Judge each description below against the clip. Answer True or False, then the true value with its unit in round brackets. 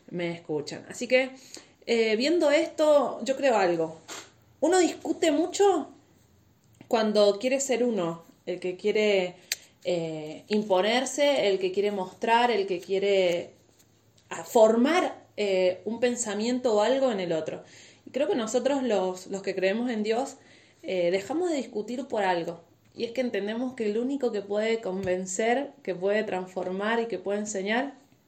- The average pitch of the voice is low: False (210 Hz)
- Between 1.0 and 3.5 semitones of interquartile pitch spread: False (5.5 semitones)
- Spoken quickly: False (150 wpm)